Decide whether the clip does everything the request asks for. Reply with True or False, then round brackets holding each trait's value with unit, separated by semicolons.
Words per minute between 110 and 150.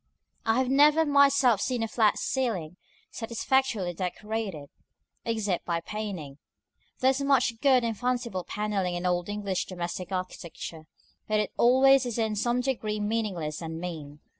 True (145 wpm)